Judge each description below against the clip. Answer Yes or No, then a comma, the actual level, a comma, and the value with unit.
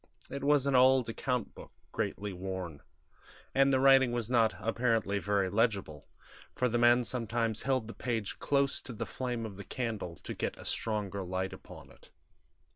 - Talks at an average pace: Yes, average, 175 wpm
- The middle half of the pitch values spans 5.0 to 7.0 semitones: No, average, 4.0 semitones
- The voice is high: No, low, 115 Hz